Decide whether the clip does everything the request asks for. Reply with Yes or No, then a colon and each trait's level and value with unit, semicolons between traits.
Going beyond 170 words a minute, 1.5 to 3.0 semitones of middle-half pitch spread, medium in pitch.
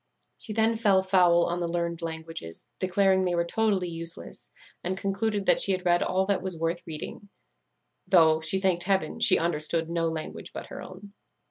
Yes: average, 185 wpm; narrow, 2.5 semitones; medium, 175 Hz